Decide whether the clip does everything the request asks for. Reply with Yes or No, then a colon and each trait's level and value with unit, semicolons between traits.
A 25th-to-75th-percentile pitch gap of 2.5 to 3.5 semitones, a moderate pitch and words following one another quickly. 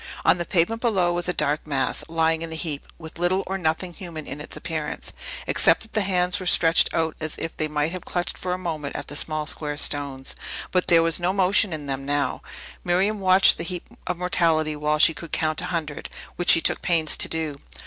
Yes: average, 2.8 semitones; medium, 165 Hz; fast, 225 wpm